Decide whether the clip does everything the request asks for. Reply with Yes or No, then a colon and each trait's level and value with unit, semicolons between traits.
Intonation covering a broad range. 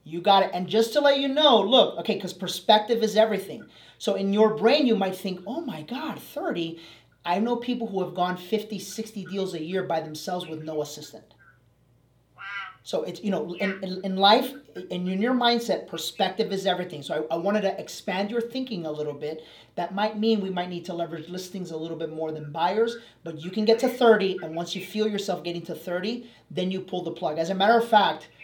No: average, 4.1 semitones